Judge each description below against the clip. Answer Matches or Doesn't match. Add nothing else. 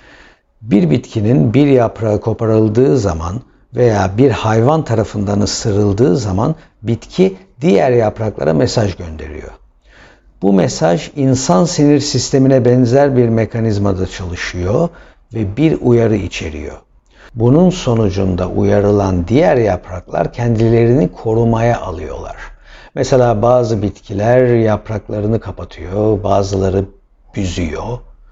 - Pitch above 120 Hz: Doesn't match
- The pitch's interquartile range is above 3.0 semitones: Matches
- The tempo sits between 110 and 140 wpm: Doesn't match